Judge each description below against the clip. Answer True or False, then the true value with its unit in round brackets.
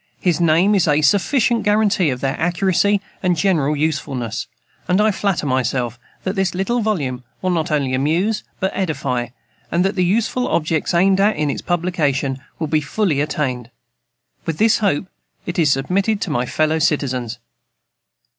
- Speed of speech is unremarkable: True (165 wpm)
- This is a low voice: False (165 Hz)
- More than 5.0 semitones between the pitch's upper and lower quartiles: True (5.6 semitones)